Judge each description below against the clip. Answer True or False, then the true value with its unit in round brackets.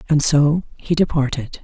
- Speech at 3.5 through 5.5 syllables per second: True (4.4 syllables/s)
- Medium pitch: True (150 Hz)